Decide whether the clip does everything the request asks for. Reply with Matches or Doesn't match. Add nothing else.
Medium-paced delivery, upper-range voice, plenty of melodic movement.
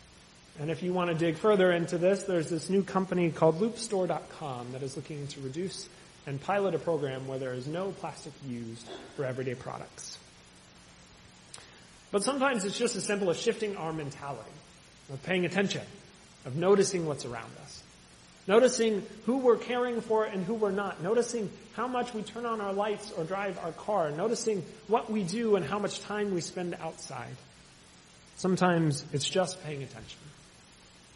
Doesn't match